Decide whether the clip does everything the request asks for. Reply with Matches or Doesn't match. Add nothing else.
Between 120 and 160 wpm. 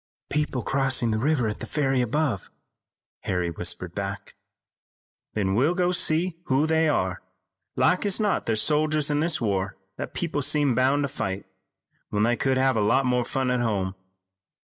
Doesn't match